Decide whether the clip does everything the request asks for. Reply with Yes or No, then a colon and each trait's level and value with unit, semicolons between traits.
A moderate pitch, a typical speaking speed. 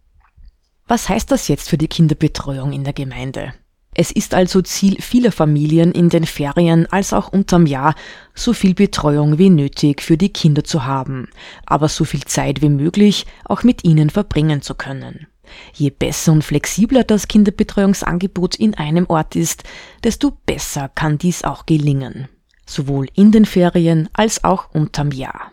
Yes: medium, 160 Hz; average, 160 wpm